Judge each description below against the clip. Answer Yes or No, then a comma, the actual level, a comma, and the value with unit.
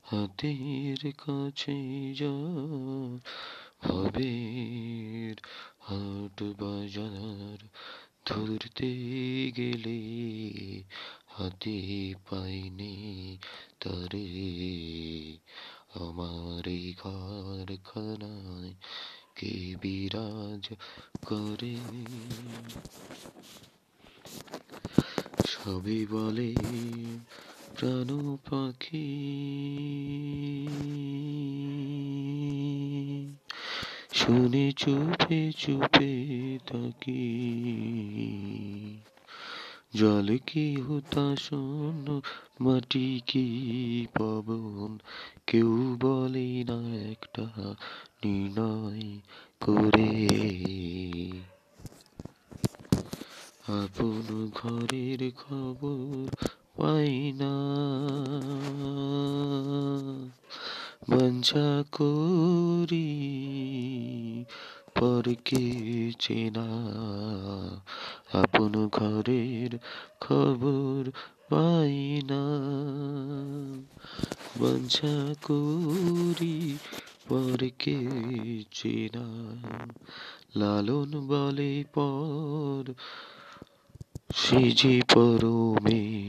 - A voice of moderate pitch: No, low, 120 Hz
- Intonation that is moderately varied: Yes, average, 4.7 semitones